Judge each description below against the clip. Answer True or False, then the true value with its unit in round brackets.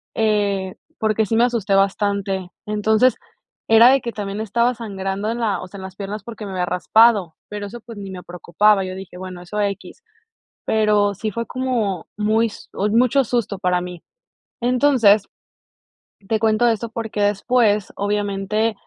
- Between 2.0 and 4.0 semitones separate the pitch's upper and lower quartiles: True (2.6 semitones)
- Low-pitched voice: False (210 Hz)